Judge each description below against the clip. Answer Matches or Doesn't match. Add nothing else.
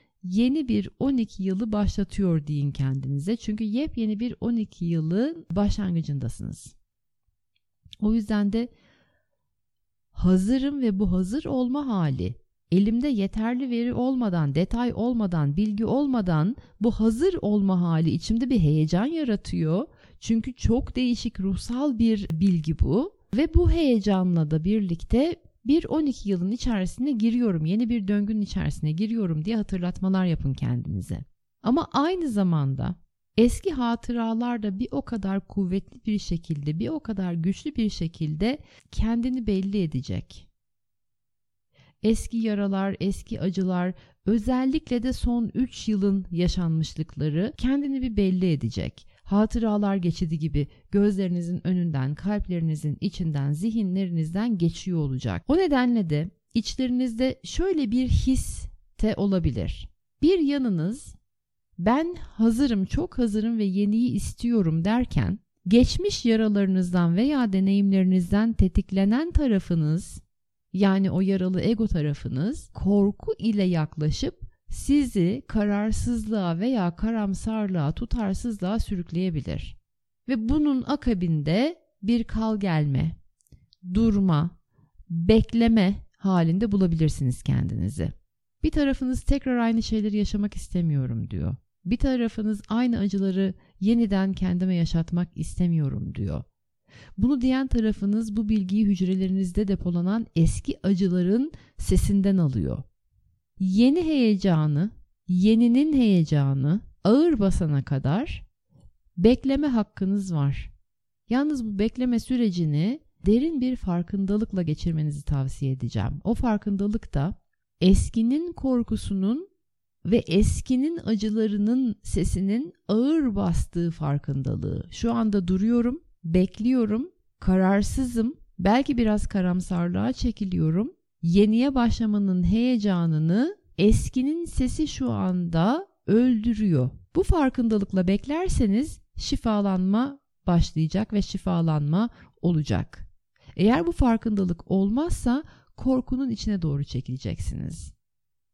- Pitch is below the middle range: Doesn't match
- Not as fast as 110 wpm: Matches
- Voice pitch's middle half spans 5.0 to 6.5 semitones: Matches